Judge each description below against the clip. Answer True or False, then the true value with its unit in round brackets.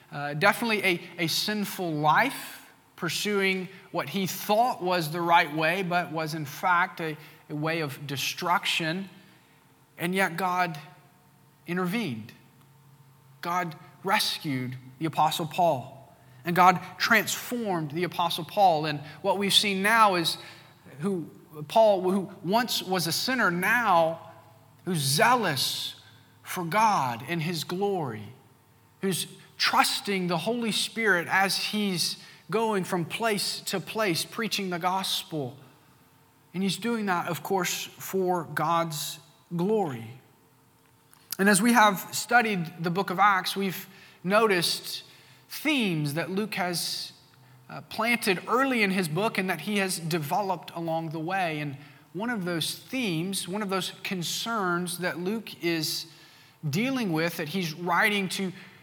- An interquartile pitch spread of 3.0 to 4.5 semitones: True (3.7 semitones)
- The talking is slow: True (130 wpm)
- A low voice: False (175 Hz)